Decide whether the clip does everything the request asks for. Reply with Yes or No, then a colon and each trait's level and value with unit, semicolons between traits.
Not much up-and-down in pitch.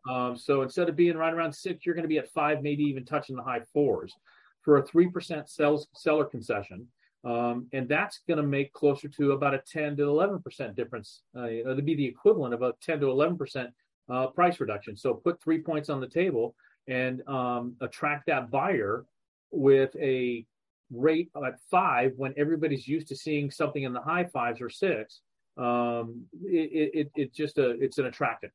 No: average, 3.7 semitones